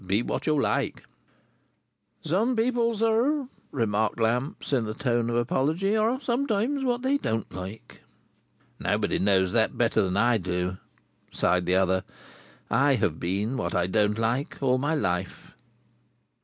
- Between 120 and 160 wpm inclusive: Yes, average, 145 wpm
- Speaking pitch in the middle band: No, low, 120 Hz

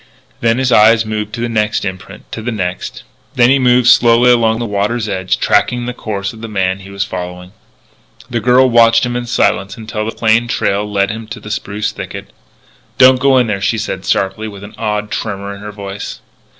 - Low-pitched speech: Yes, low, 110 Hz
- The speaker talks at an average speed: No, fast, 210 wpm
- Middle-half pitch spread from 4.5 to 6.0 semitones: No, average, 3.0 semitones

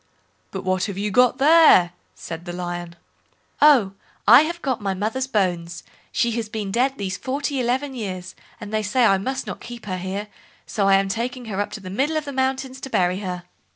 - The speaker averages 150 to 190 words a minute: No, fast, 205 wpm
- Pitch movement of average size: No, wide, 5.7 semitones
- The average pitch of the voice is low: No, high, 215 Hz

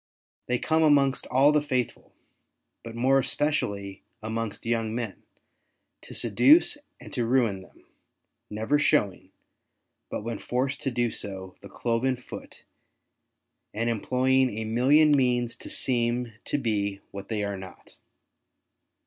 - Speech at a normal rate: No, slow, 130 wpm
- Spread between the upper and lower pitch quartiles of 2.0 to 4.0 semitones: Yes, average, 3.4 semitones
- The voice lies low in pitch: Yes, low, 120 Hz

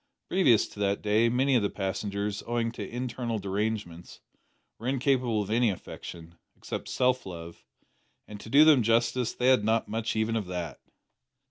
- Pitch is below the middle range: Yes, low, 110 Hz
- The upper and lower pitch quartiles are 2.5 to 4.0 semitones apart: Yes, average, 3.4 semitones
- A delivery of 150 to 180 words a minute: Yes, average, 165 wpm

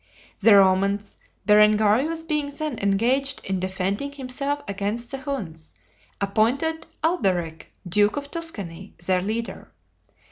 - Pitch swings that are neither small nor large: No, wide, 6.3 semitones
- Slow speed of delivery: Yes, slow, 110 wpm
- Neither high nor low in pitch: No, high, 215 Hz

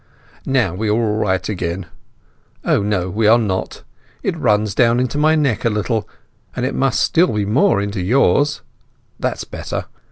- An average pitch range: Yes, average, 4.1 semitones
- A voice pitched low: Yes, low, 110 Hz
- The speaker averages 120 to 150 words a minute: No, average, 160 wpm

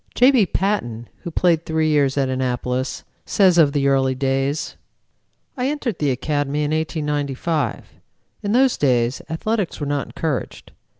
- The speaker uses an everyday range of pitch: Yes, average, 4.2 semitones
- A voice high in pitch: No, medium, 150 Hz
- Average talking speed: Yes, average, 145 wpm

